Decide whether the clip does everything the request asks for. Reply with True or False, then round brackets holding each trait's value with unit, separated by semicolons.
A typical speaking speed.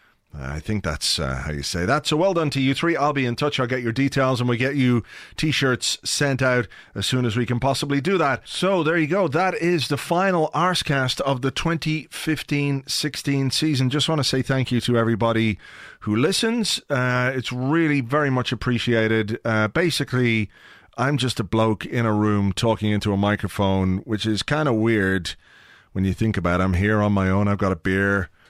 False (210 wpm)